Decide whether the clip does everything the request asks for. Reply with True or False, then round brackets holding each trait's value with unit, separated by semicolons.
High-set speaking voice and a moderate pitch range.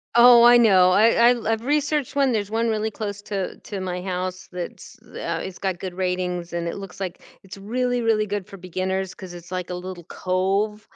True (195 Hz; 3.5 semitones)